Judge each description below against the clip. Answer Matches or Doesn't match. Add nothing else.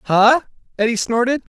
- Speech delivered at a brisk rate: Doesn't match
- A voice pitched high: Matches